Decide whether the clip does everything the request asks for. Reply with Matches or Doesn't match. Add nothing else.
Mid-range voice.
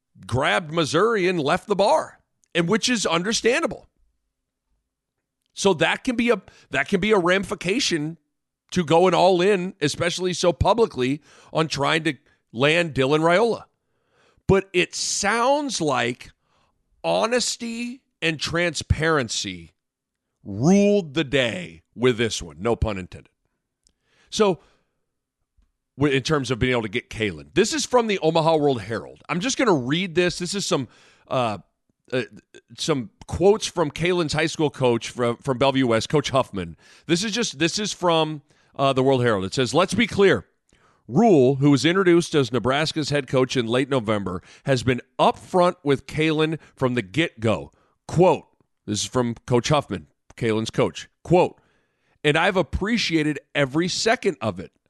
Matches